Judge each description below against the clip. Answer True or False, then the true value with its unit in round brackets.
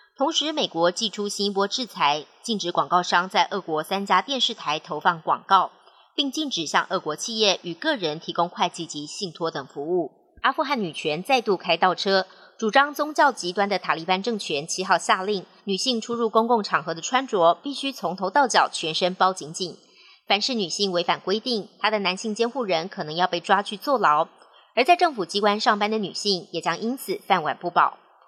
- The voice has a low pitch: False (195 Hz)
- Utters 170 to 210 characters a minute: False (295 characters per minute)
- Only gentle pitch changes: False (5.2 semitones)